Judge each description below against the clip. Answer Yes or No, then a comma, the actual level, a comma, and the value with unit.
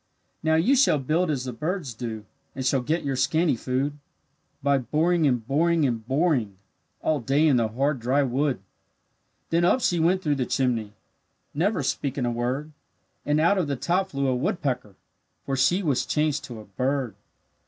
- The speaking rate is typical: Yes, average, 180 wpm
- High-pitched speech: No, medium, 140 Hz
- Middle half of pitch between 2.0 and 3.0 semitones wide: No, average, 4.1 semitones